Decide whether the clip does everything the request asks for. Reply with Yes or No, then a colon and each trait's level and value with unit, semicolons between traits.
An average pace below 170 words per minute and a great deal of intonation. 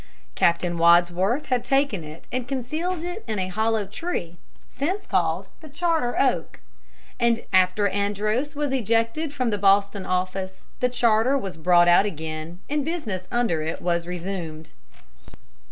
Yes: average, 140 wpm; wide, 6.8 semitones